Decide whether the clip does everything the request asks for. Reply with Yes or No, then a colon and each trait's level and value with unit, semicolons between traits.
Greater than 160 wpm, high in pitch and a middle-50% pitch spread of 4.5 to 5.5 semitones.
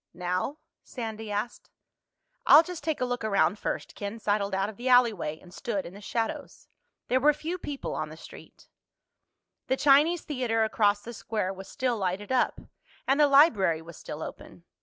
Yes: average, 180 wpm; high, 225 Hz; average, 4.8 semitones